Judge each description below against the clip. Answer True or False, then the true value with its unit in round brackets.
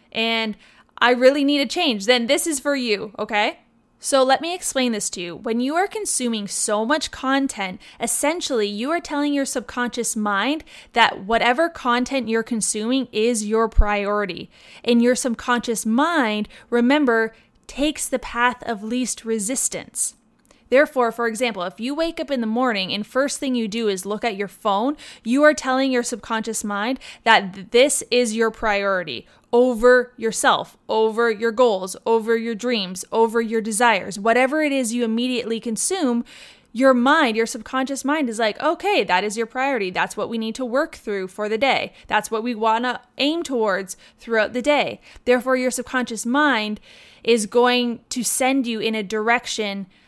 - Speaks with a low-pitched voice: False (240 Hz)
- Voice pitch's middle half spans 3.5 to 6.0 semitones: False (2.9 semitones)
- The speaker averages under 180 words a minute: True (170 wpm)